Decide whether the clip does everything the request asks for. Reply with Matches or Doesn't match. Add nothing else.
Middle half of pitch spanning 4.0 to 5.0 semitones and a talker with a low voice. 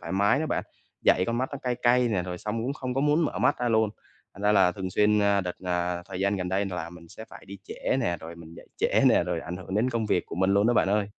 Matches